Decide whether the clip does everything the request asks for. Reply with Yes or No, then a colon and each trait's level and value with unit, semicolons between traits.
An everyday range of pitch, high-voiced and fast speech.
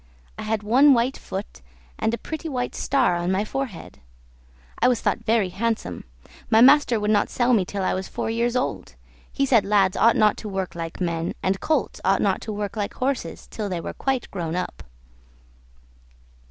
No: average, 4.6 semitones; high, 215 Hz; average, 195 wpm